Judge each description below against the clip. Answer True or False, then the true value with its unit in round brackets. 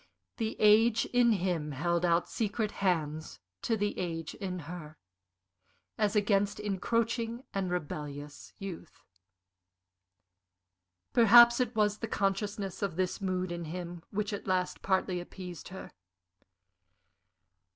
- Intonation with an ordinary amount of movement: True (3.5 semitones)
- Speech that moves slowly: True (120 wpm)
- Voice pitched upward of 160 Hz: True (190 Hz)